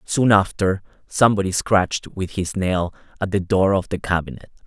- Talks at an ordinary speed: Yes, average, 165 wpm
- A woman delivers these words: No, male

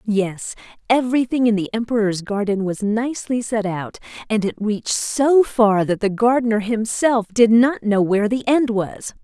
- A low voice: No, high, 220 Hz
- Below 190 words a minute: Yes, average, 170 wpm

